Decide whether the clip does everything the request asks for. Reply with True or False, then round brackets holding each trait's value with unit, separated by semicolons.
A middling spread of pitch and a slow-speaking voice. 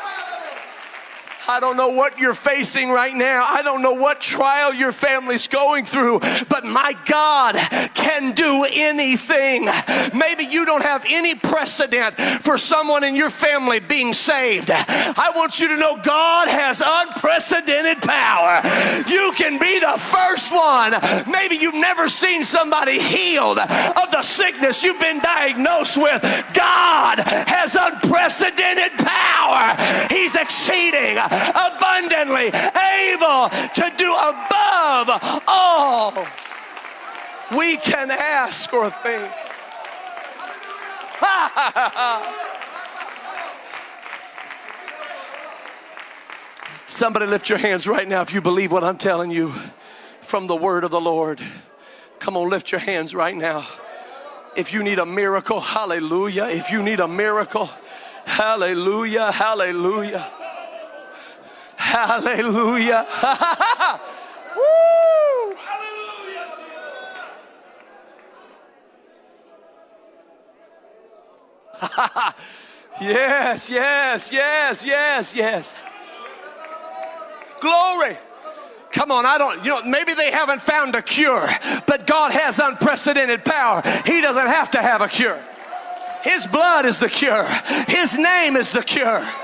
False (5.7 semitones; 110 wpm)